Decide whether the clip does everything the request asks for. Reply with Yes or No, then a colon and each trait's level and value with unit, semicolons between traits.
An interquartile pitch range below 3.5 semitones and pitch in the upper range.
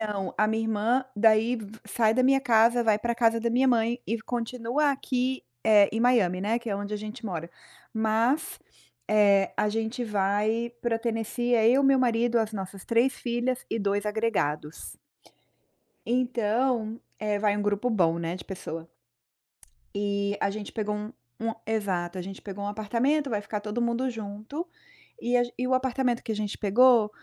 Yes: average, 2.8 semitones; high, 220 Hz